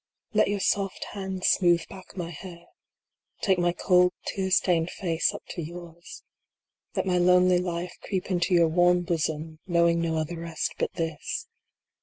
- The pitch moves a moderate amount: No, narrow, 1.5 semitones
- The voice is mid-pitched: Yes, medium, 175 Hz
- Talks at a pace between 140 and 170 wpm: Yes, average, 165 wpm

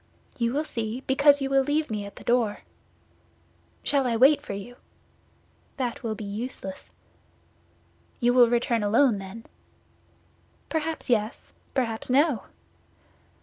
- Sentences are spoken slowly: Yes, slow, 130 wpm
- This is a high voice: Yes, high, 245 Hz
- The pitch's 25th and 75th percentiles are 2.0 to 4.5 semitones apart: Yes, average, 3.7 semitones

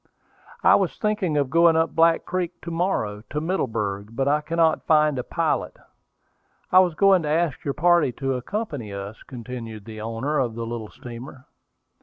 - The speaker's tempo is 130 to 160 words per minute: No, average, 175 wpm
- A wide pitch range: Yes, wide, 6.2 semitones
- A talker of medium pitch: Yes, medium, 150 Hz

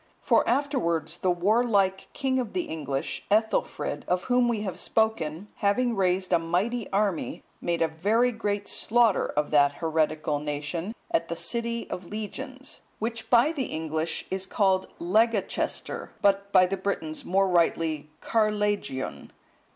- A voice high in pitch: Yes, high, 195 Hz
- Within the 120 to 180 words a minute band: Yes, average, 145 wpm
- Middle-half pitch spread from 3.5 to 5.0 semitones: No, wide, 5.4 semitones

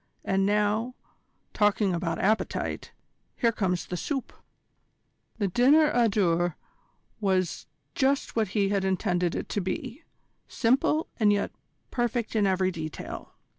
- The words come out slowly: Yes, slow, 130 wpm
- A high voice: Yes, high, 205 Hz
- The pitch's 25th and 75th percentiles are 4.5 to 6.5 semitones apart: No, average, 4.0 semitones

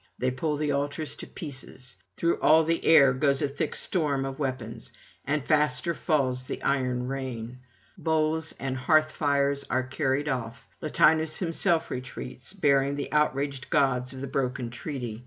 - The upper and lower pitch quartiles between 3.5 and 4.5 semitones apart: No, average, 3.1 semitones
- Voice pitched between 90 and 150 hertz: Yes, medium, 140 Hz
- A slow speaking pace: No, average, 155 wpm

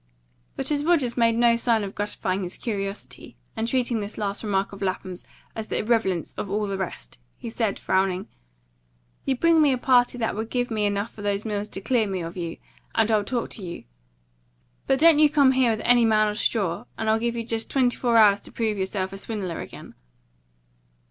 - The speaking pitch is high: Yes, high, 220 Hz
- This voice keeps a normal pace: No, fast, 215 wpm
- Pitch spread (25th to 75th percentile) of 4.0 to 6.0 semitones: No, average, 3.3 semitones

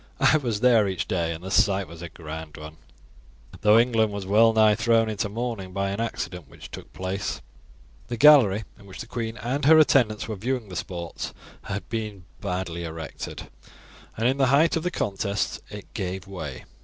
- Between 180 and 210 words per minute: Yes, average, 190 wpm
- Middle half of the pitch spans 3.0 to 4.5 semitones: Yes, average, 3.9 semitones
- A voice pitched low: Yes, low, 105 Hz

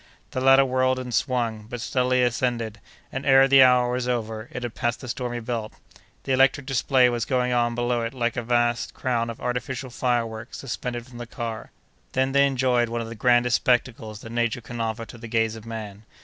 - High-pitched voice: No, low, 120 Hz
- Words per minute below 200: No, fast, 205 wpm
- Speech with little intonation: Yes, narrow, 1.8 semitones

